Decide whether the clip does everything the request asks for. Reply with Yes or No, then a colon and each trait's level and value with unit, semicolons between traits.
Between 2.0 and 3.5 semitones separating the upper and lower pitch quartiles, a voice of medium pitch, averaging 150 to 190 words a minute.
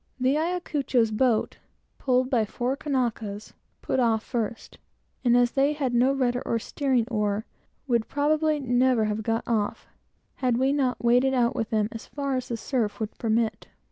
No: average, 3.1 semitones; high, 245 Hz; average, 170 wpm